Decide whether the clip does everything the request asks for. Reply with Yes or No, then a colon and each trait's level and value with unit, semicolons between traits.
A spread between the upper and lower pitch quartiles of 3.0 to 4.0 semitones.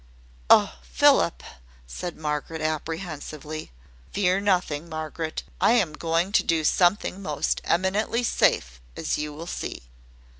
Yes: average, 3.3 semitones